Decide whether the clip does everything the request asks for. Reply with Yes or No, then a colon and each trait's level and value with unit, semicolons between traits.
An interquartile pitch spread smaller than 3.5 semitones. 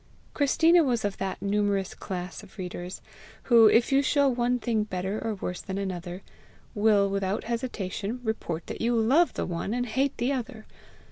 No: average, 4.2 semitones